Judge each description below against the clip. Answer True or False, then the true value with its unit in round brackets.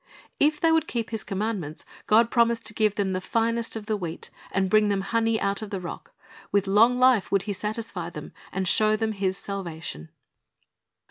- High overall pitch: True (210 Hz)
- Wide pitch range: False (3.0 semitones)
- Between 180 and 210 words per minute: True (200 wpm)